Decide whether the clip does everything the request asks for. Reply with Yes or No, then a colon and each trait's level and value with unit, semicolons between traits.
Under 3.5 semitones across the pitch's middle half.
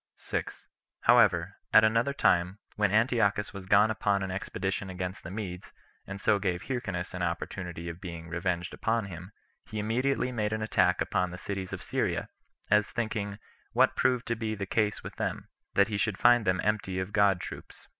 Yes: average, 3.0 semitones